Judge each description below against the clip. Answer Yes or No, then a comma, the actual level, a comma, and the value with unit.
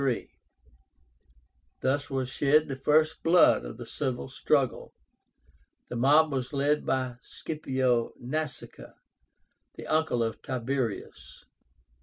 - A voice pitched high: No, low, 135 Hz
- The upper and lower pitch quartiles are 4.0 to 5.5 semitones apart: No, average, 3.0 semitones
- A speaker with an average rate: No, slow, 105 wpm